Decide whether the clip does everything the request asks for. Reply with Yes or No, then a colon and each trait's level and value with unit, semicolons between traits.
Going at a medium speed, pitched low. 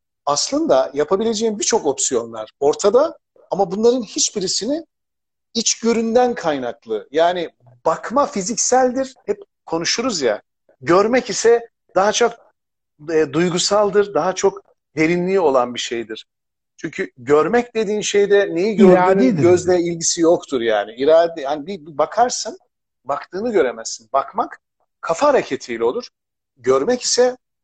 No: average, 110 wpm; high, 195 Hz